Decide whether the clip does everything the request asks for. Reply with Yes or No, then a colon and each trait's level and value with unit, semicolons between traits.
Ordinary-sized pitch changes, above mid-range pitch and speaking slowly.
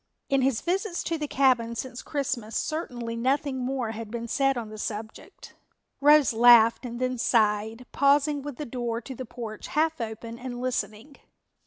No: average, 3.3 semitones; high, 245 Hz; average, 170 wpm